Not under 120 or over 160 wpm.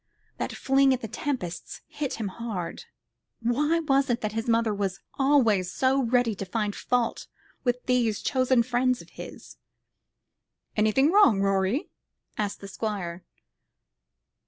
Yes: slow, 135 wpm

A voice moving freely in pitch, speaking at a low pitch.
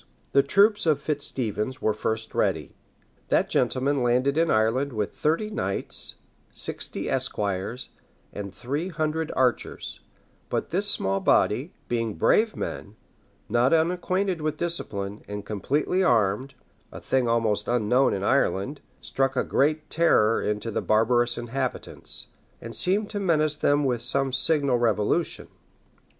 Yes: wide, 5.8 semitones; low, 130 Hz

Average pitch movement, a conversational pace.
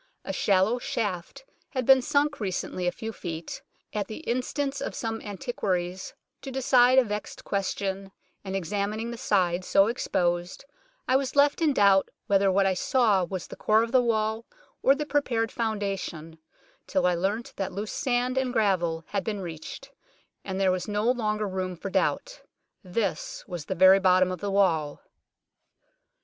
Yes: average, 4.6 semitones; average, 170 wpm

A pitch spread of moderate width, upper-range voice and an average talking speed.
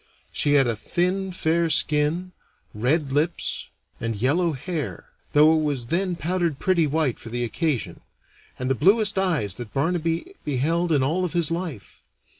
No: average, 4.5 semitones; medium, 155 Hz; average, 160 wpm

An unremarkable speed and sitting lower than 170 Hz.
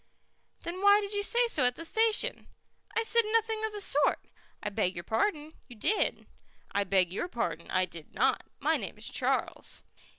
No: average, 190 wpm; very high, 330 Hz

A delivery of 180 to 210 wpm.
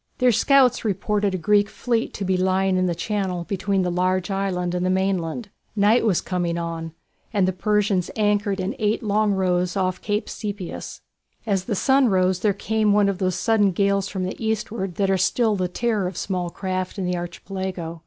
Yes: average, 195 wpm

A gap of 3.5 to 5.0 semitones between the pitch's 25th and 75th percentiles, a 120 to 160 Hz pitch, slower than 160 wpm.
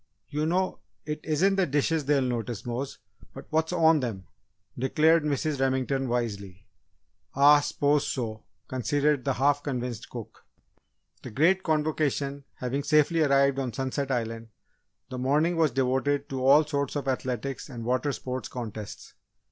No: average, 3.1 semitones; medium, 140 Hz; average, 145 wpm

